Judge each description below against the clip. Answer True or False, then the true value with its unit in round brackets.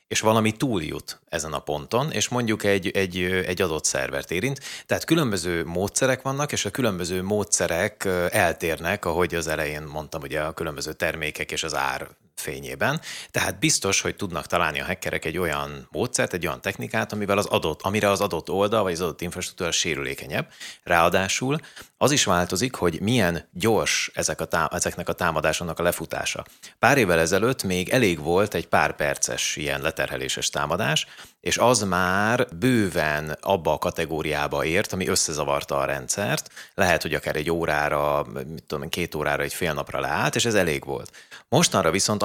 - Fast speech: True (165 wpm)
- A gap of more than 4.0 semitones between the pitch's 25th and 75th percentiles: True (4.4 semitones)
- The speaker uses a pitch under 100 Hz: True (90 Hz)